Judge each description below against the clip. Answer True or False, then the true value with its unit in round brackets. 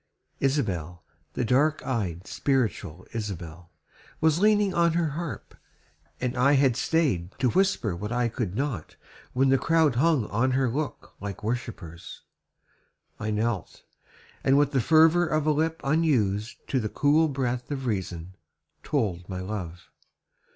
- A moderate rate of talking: True (145 wpm)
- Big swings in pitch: True (6.8 semitones)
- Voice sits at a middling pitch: False (125 Hz)